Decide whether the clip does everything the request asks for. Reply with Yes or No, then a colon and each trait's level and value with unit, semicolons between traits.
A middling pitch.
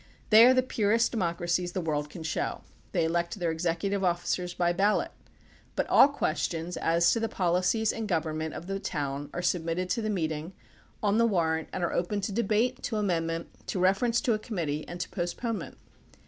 Yes: medium, 180 Hz